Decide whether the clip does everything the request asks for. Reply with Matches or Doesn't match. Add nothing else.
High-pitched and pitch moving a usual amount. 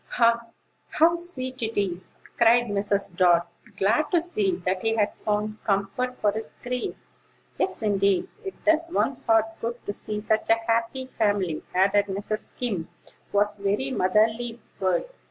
Matches